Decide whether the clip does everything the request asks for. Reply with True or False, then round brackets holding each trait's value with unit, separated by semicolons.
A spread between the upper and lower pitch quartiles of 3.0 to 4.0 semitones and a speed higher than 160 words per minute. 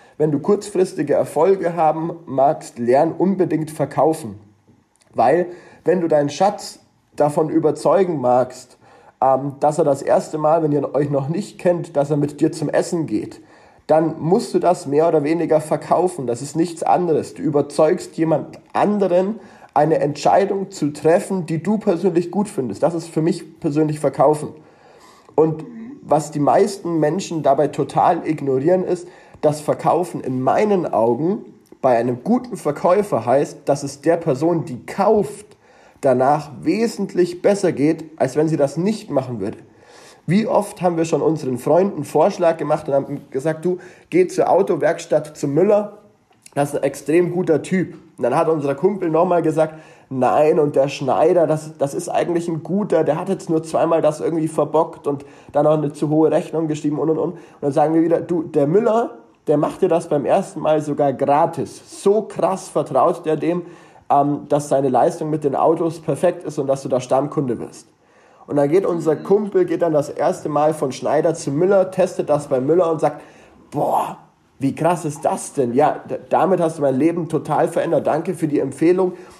True (3.3 semitones; 180 wpm)